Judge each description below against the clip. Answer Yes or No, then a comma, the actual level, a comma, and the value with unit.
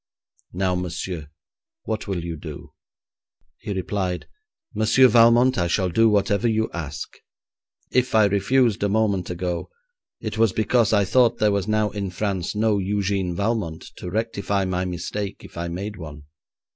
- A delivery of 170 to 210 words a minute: No, average, 155 wpm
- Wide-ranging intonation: No, average, 3.4 semitones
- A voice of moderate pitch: No, low, 100 Hz